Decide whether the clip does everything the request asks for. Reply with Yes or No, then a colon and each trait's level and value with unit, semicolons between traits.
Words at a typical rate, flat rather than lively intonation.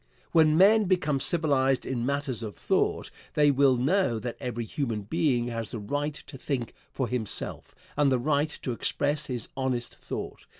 No: average, 170 wpm; average, 3.7 semitones